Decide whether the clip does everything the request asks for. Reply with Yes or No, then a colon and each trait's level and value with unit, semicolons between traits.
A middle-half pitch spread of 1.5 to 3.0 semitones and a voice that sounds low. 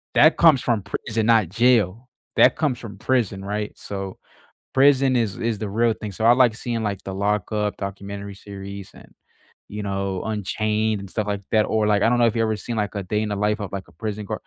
Yes: narrow, 2.5 semitones; low, 105 Hz